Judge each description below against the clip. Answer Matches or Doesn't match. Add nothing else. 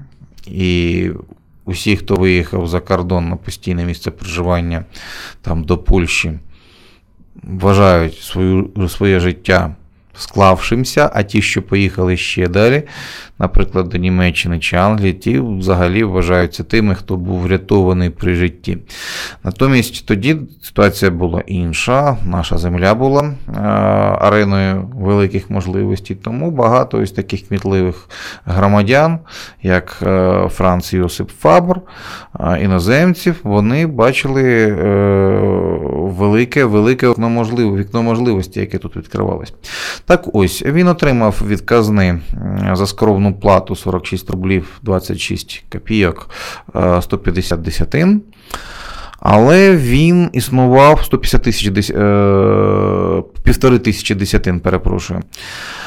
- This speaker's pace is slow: Matches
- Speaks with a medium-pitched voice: Doesn't match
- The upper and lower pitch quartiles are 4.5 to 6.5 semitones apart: Doesn't match